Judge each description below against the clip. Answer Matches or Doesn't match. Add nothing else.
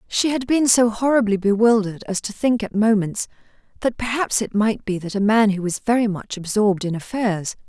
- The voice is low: Doesn't match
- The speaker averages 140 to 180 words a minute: Doesn't match